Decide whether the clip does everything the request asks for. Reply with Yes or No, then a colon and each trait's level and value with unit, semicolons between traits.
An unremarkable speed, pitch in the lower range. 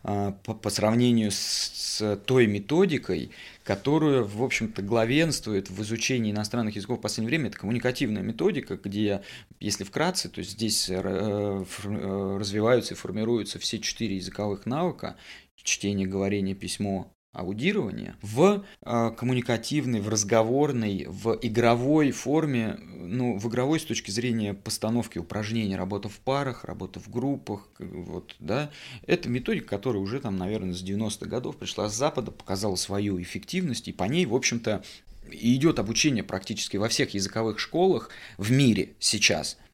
Yes: average, 135 wpm; low, 110 Hz